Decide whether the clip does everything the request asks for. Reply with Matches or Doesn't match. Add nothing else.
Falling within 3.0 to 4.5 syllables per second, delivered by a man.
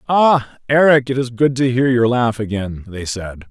Matches